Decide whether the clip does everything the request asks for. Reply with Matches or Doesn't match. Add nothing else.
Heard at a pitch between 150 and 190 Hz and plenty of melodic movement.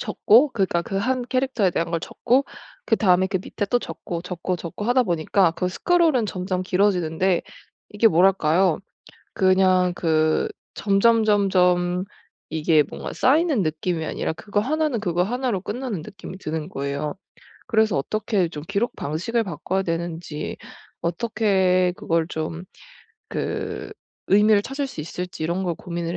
Doesn't match